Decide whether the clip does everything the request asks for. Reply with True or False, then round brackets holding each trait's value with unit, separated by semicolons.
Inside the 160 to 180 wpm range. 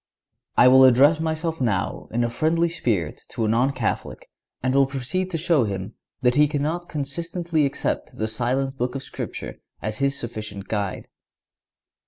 True (165 wpm)